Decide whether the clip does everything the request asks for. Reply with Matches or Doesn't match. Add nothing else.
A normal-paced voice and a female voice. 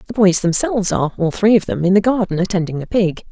Doesn't match